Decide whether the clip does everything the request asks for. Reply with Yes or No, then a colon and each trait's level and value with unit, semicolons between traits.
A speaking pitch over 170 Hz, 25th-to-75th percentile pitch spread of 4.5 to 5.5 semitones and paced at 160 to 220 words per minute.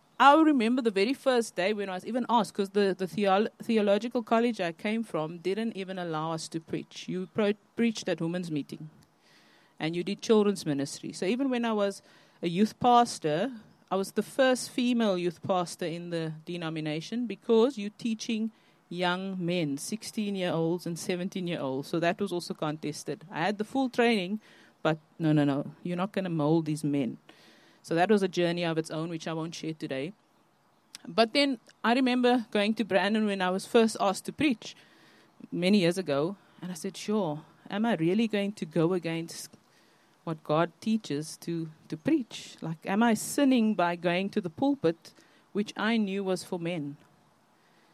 Yes: high, 190 Hz; average, 5.1 semitones; average, 190 wpm